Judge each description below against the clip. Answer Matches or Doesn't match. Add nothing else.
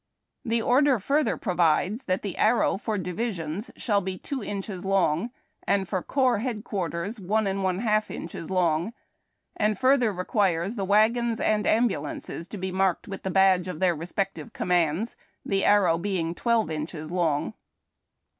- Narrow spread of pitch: Doesn't match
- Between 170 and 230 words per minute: Doesn't match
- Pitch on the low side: Doesn't match